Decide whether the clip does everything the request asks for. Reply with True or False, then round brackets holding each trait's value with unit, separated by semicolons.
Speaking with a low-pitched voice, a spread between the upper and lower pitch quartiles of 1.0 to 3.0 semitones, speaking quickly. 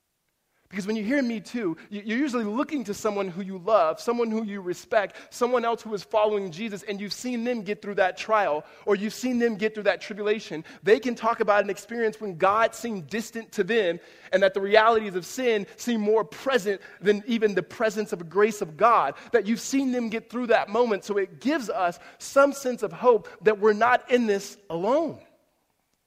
False (215 Hz; 2.6 semitones; 210 wpm)